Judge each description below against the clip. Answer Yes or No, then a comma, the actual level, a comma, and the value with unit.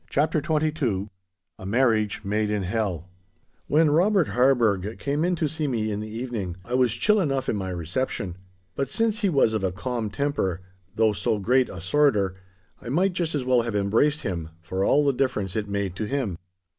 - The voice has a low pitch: Yes, low, 115 Hz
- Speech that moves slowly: No, average, 195 wpm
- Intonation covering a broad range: Yes, wide, 6.3 semitones